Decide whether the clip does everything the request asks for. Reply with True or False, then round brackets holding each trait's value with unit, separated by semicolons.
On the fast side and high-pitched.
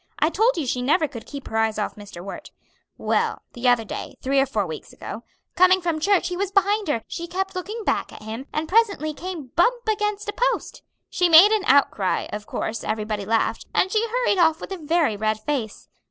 True (220 wpm; 310 Hz)